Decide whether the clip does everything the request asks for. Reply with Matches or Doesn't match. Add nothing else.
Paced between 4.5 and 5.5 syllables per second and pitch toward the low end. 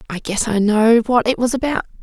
Doesn't match